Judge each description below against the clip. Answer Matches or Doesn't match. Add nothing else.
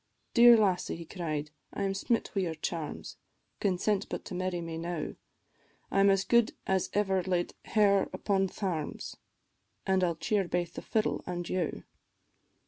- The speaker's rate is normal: Matches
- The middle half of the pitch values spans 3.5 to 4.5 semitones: Doesn't match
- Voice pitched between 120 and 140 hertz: Doesn't match